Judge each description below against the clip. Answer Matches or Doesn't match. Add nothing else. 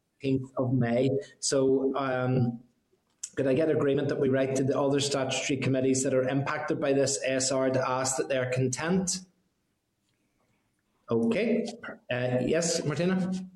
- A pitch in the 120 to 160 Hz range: Matches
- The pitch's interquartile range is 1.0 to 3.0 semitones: Matches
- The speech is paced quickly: Doesn't match